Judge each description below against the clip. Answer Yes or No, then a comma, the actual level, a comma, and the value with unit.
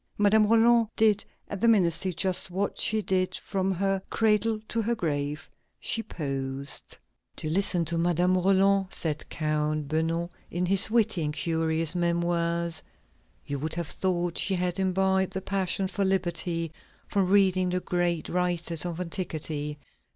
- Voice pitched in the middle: Yes, medium, 180 Hz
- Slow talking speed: No, average, 150 wpm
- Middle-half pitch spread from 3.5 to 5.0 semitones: No, average, 2.9 semitones